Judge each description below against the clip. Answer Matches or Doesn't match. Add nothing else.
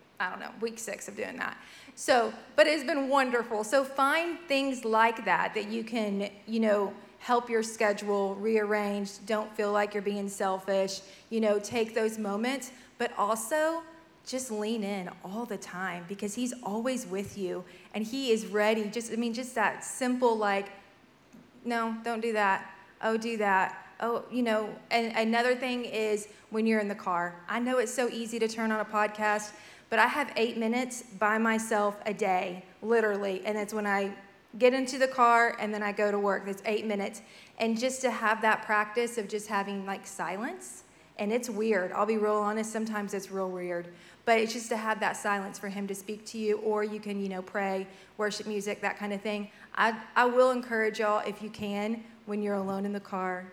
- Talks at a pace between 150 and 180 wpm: Doesn't match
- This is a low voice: Doesn't match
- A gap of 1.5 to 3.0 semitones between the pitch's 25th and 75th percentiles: Matches